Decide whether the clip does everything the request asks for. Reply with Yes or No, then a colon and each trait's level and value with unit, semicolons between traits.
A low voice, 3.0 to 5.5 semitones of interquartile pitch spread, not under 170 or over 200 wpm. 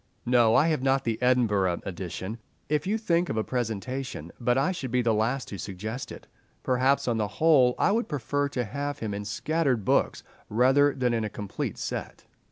Yes: low, 125 Hz; average, 4.6 semitones; average, 190 wpm